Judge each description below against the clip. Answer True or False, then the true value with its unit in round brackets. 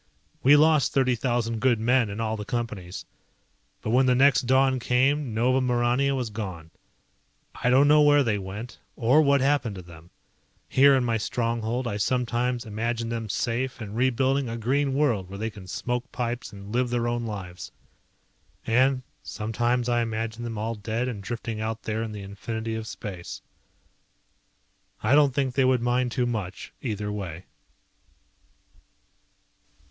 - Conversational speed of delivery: True (165 wpm)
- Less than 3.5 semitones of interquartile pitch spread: True (2.9 semitones)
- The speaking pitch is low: True (120 Hz)